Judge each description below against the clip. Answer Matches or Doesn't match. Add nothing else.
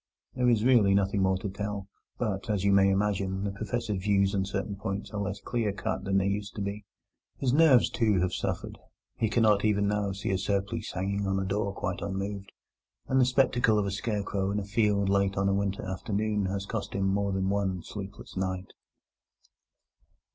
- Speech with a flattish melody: Matches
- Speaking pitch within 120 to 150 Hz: Doesn't match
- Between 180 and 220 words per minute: Matches